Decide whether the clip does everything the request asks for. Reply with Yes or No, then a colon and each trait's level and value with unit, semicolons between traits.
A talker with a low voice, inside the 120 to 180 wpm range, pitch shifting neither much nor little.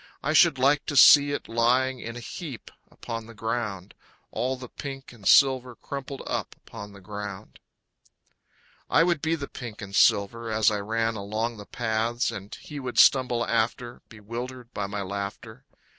Yes: low, 115 Hz; average, 170 wpm; average, 3.6 semitones